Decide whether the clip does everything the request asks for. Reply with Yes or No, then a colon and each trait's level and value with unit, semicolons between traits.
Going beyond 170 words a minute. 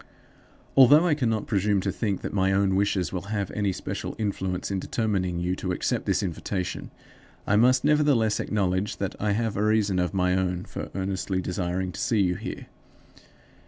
Yes: average, 180 wpm